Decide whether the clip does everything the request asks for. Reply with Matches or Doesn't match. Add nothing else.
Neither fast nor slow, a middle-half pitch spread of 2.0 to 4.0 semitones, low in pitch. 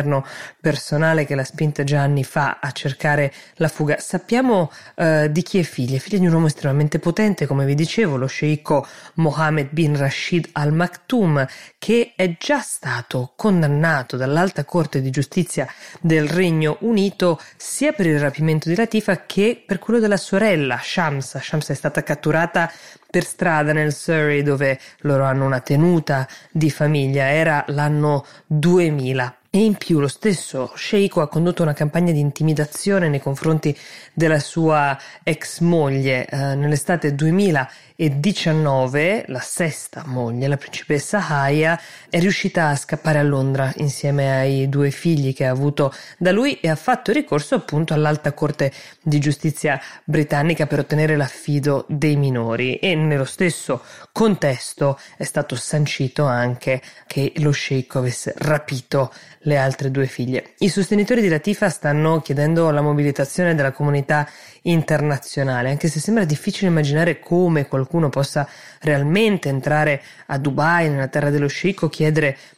Doesn't match